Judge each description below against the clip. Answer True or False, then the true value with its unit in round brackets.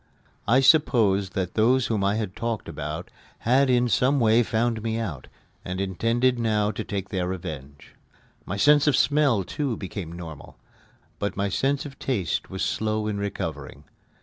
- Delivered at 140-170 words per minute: True (165 wpm)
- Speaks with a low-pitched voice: True (110 Hz)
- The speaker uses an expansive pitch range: False (4.4 semitones)